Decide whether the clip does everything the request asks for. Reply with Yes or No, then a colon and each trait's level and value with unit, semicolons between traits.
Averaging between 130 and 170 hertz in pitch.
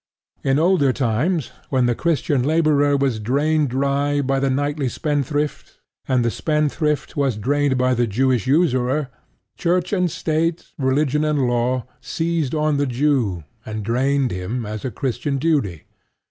Yes: medium, 140 Hz